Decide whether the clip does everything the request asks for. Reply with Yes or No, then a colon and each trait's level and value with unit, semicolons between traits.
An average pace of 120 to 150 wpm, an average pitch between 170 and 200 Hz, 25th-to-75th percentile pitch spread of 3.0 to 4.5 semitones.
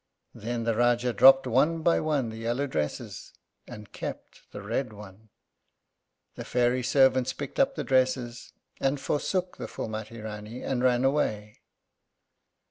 No: average, 140 wpm; low, 125 Hz; average, 3.4 semitones